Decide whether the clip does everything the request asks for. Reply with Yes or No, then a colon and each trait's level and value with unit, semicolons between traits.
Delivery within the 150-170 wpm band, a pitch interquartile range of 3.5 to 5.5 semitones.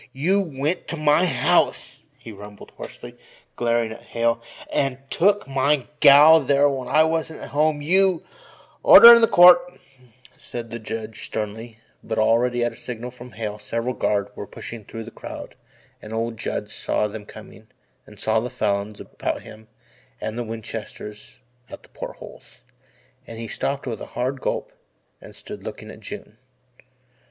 Yes: average, 165 wpm; average, 4.7 semitones